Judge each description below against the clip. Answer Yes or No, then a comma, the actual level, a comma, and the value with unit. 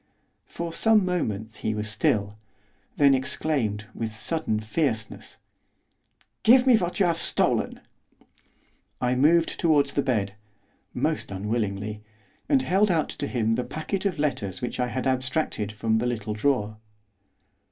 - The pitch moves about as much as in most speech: No, wide, 6.9 semitones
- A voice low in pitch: Yes, low, 125 Hz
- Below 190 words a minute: Yes, average, 140 wpm